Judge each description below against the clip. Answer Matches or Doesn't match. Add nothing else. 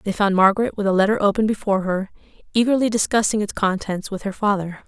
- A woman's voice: Matches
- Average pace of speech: Matches